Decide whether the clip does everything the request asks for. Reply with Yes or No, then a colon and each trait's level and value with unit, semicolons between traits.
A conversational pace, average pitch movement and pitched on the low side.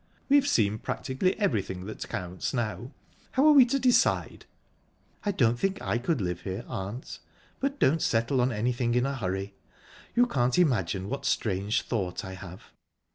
No: average, 160 wpm; wide, 8.8 semitones; low, 120 Hz